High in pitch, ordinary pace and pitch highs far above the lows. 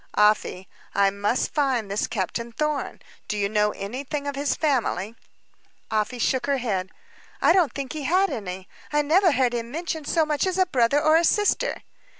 Yes: very high, 265 Hz; average, 180 wpm; wide, 6.3 semitones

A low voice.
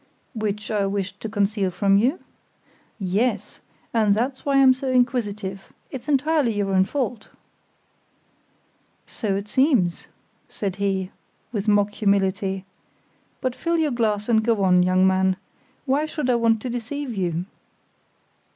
No: high, 210 Hz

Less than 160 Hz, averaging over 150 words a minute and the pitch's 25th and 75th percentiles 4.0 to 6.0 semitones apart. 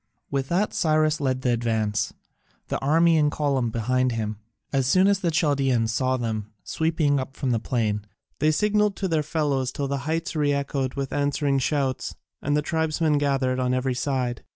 No: medium, 140 Hz; average, 180 wpm; average, 3.3 semitones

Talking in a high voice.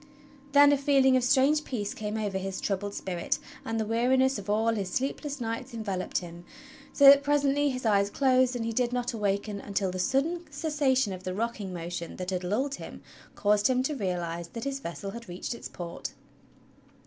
Yes: high, 225 Hz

